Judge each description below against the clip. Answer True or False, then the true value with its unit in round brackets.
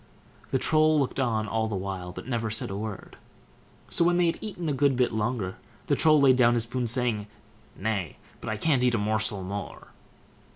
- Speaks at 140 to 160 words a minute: False (205 wpm)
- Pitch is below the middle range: True (120 Hz)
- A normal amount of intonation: True (4.3 semitones)